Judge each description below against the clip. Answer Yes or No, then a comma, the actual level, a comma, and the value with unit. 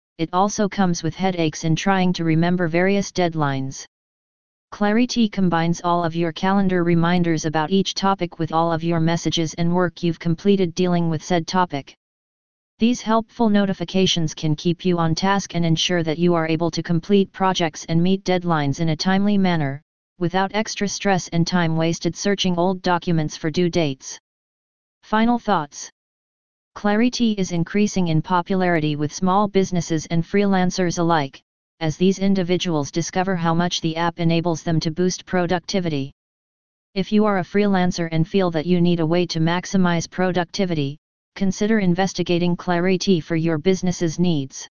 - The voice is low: No, medium, 175 Hz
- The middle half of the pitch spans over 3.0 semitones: No, narrow, 2.5 semitones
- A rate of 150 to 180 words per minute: Yes, average, 160 wpm